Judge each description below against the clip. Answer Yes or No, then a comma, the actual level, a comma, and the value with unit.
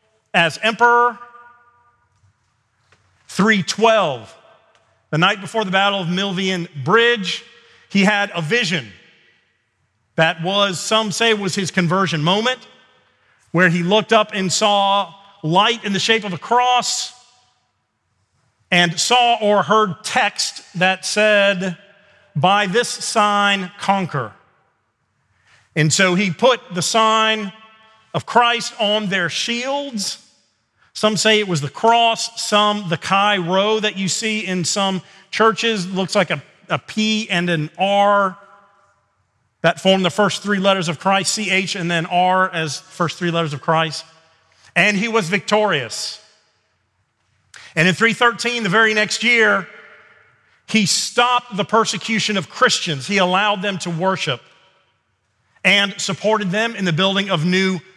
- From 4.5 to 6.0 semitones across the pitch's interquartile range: No, average, 4.1 semitones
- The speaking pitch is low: No, high, 195 Hz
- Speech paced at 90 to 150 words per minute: Yes, slow, 135 wpm